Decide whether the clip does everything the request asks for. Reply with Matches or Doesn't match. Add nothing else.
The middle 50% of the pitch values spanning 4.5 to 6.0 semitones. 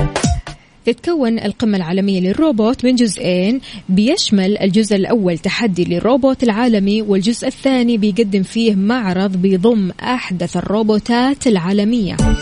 Doesn't match